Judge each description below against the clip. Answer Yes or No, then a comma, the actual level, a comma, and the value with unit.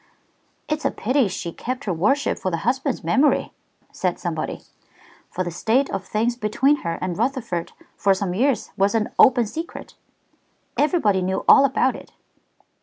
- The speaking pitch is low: No, high, 225 Hz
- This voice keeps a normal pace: Yes, average, 160 wpm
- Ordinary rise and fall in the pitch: No, wide, 6.1 semitones